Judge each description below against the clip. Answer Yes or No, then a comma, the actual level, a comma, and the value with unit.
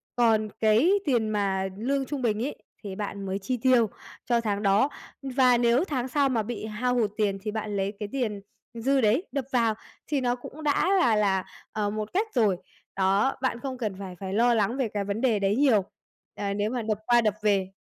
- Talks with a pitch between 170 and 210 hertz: No, high, 220 Hz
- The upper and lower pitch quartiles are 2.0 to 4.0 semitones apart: Yes, average, 3.7 semitones